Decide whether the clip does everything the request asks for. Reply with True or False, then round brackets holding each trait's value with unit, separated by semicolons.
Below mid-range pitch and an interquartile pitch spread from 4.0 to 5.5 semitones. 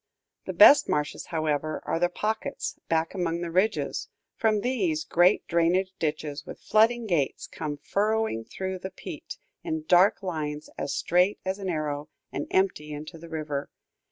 False (170 Hz; 4.3 semitones)